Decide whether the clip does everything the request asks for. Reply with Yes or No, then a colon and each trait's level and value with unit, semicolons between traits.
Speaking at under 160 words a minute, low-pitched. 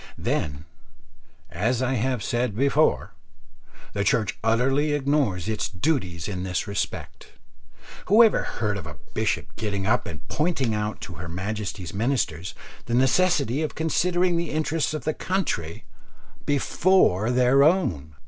Yes: slow, 135 wpm; low, 120 Hz